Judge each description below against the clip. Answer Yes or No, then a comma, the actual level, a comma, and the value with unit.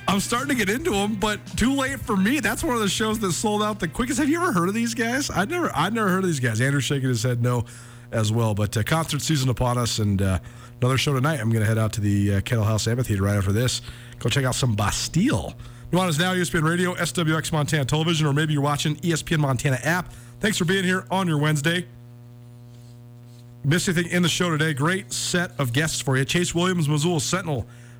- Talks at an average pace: No, fast, 240 wpm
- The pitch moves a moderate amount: No, wide, 7.0 semitones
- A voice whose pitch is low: No, medium, 150 Hz